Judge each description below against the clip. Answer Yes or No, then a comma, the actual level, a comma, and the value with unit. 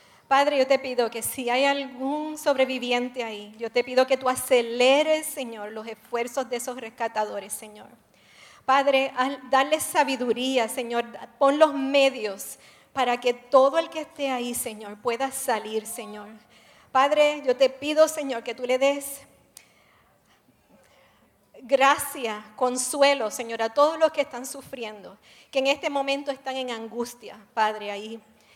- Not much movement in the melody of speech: No, average, 3.1 semitones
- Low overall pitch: No, very high, 255 Hz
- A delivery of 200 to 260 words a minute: No, average, 145 wpm